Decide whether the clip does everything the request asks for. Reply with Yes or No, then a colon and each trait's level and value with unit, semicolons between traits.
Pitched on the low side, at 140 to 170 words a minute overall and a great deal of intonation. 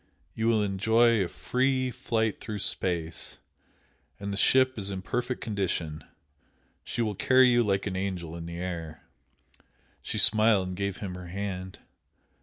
No: low, 100 Hz; average, 155 wpm; average, 3.8 semitones